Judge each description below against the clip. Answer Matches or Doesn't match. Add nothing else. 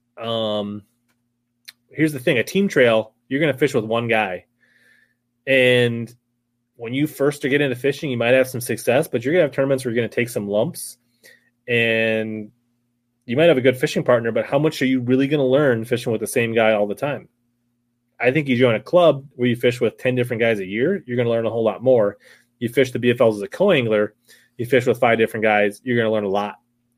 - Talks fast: Matches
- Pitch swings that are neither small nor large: Doesn't match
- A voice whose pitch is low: Matches